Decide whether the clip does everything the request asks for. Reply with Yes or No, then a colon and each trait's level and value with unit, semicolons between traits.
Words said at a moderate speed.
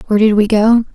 No: fast, 255 wpm